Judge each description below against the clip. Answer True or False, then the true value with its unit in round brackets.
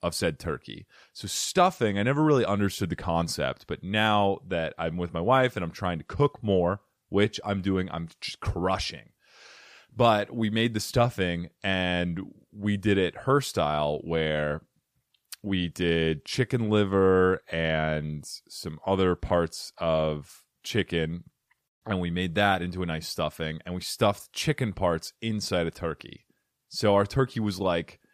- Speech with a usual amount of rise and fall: True (3.9 semitones)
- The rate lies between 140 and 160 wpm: True (155 wpm)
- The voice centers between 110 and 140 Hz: False (95 Hz)